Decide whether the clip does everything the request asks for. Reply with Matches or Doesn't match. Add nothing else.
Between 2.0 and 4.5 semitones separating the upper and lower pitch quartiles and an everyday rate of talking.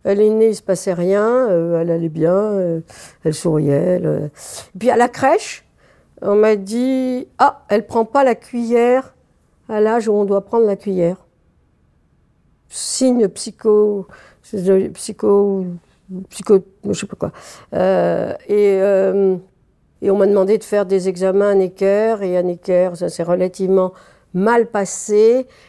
Matches